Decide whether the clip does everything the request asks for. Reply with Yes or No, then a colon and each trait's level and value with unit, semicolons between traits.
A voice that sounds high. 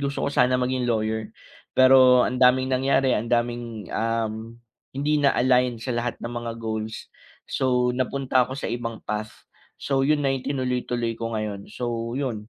No: low, 125 Hz